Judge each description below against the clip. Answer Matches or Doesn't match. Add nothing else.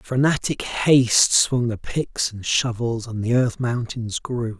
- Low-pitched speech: Matches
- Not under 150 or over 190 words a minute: Matches